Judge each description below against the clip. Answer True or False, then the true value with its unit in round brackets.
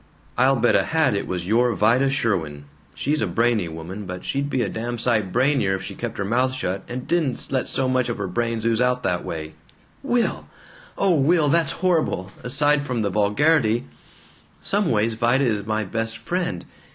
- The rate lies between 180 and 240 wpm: True (190 wpm)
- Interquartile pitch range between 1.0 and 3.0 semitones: False (5.0 semitones)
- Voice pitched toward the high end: False (120 Hz)